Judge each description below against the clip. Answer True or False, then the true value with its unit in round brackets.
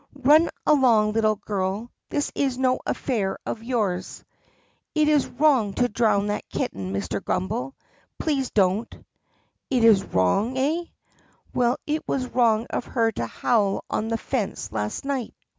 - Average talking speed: True (150 wpm)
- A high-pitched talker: True (230 Hz)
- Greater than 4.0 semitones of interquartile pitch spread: True (4.6 semitones)